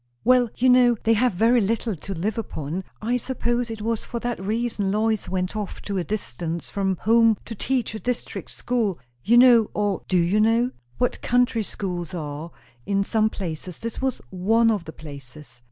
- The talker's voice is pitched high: Yes, high, 215 Hz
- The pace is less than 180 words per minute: No, average, 185 wpm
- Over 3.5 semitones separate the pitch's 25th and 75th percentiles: Yes, average, 4.4 semitones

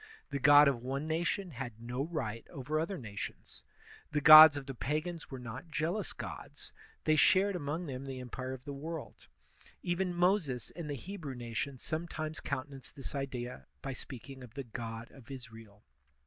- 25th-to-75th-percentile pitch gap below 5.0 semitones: Yes, average, 4.0 semitones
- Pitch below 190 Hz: Yes, medium, 140 Hz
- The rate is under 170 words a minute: No, average, 175 wpm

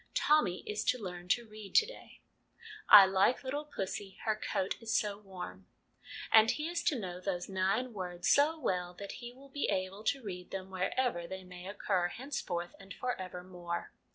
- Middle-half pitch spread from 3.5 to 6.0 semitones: Yes, wide, 5.5 semitones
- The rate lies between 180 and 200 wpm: Yes, average, 190 wpm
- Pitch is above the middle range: Yes, high, 195 Hz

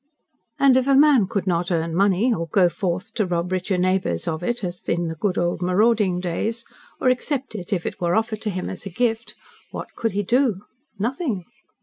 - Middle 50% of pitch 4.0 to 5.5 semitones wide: Yes, average, 4.6 semitones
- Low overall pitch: No, high, 195 Hz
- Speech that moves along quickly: Yes, fast, 210 wpm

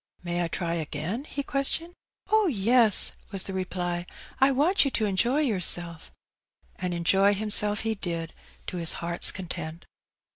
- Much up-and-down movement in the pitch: Yes, wide, 5.9 semitones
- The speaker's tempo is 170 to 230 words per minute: No, average, 155 wpm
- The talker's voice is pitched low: No, high, 190 Hz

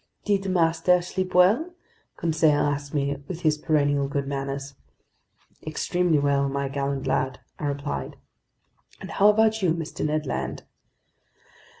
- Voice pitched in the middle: Yes, medium, 150 Hz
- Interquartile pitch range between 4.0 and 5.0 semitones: Yes, average, 4.4 semitones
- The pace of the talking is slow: Yes, slow, 130 wpm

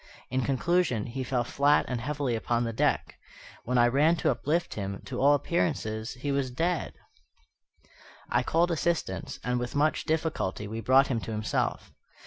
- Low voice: Yes, low, 130 Hz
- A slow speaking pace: No, average, 165 wpm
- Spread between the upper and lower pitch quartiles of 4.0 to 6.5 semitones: Yes, average, 4.3 semitones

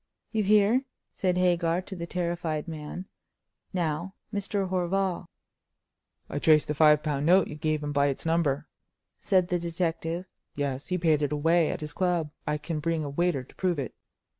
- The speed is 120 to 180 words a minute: Yes, average, 175 wpm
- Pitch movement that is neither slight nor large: Yes, average, 3.2 semitones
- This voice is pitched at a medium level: Yes, medium, 165 Hz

